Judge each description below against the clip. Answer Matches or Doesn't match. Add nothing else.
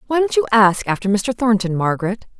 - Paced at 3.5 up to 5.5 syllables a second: Doesn't match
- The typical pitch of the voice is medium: Doesn't match